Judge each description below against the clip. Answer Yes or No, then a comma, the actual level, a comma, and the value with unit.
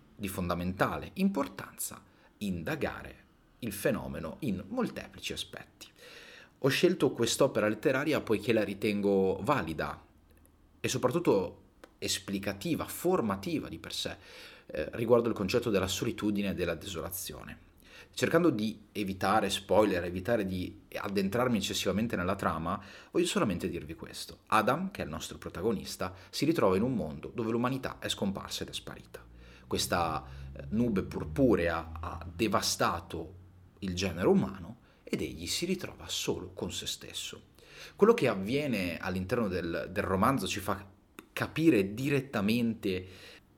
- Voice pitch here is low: Yes, low, 100 Hz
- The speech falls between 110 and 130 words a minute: Yes, average, 125 wpm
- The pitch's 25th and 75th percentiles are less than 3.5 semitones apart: No, average, 4.3 semitones